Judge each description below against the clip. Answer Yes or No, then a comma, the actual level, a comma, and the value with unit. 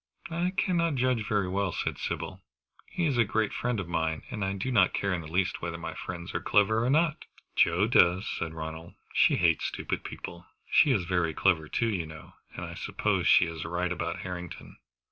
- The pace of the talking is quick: Yes, fast, 210 wpm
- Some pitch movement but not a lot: Yes, average, 4.8 semitones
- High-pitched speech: No, very low, 90 Hz